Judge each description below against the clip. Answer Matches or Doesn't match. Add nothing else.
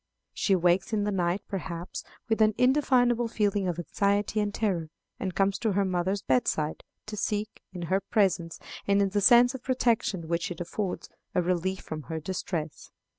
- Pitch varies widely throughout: Doesn't match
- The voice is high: Matches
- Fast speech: Doesn't match